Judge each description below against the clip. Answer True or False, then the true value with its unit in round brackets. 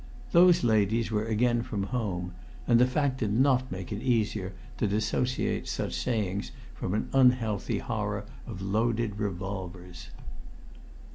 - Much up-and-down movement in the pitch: False (3.5 semitones)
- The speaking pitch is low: True (110 Hz)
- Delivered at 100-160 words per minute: True (135 wpm)